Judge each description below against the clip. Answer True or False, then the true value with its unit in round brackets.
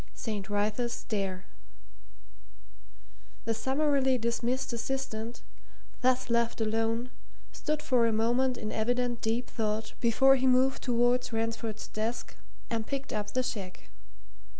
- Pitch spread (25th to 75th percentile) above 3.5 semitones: False (2.5 semitones)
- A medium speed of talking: False (120 wpm)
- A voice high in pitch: True (235 Hz)